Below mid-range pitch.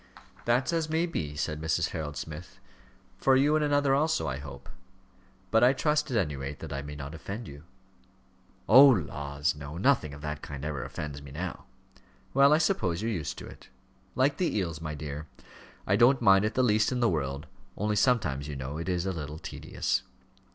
Yes: very low, 85 Hz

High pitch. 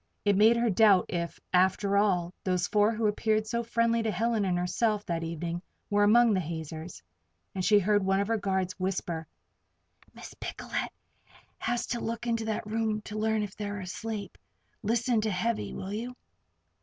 Yes: high, 210 Hz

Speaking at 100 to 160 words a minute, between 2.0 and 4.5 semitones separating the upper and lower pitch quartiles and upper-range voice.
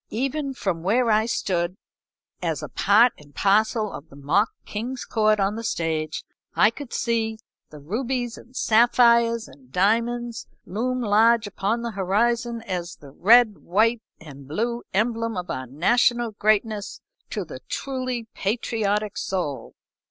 Yes: average, 145 wpm; average, 3.8 semitones; high, 220 Hz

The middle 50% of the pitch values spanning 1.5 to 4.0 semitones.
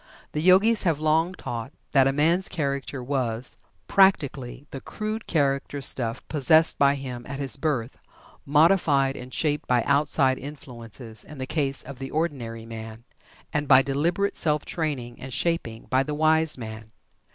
Yes: average, 3.7 semitones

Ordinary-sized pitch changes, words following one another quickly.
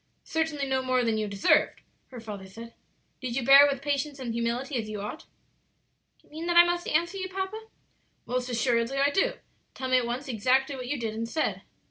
Yes: average, 4.1 semitones; fast, 215 wpm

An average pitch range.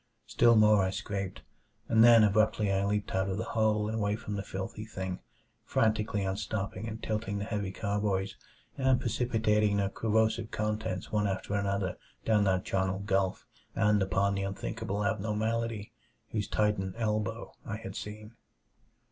No: narrow, 1.9 semitones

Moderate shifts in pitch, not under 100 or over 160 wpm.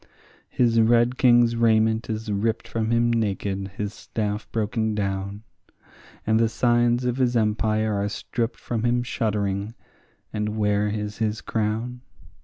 No: narrow, 1.9 semitones; average, 140 wpm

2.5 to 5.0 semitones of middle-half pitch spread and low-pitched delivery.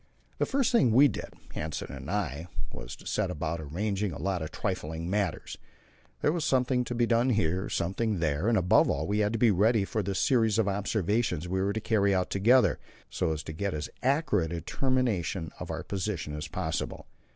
No: wide, 5.6 semitones; low, 100 Hz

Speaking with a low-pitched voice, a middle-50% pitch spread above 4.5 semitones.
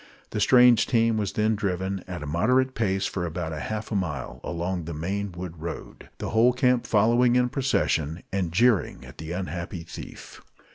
Yes: very low, 95 Hz; average, 5.1 semitones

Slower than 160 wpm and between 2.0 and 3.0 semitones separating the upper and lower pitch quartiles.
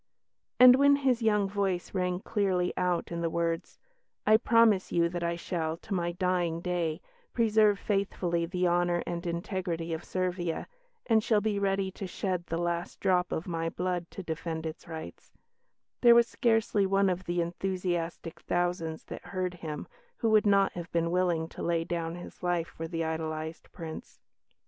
No: average, 175 wpm; average, 2.7 semitones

